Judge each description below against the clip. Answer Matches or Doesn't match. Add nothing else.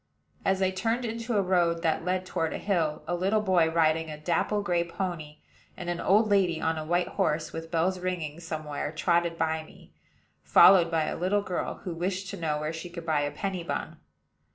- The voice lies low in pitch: Doesn't match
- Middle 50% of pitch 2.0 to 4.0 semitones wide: Matches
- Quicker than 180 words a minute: Matches